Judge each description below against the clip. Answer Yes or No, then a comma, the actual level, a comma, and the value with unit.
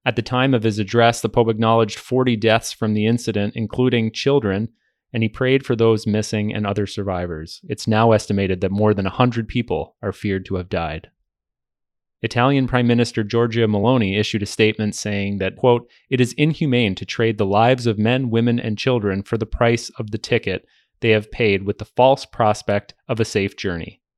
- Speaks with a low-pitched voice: Yes, low, 115 Hz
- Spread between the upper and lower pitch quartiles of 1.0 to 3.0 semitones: Yes, narrow, 2.6 semitones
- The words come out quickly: No, average, 195 wpm